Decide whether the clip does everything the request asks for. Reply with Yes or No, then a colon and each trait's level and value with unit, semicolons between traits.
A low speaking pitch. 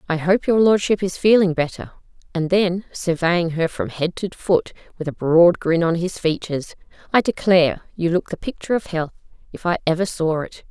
No: medium, 175 Hz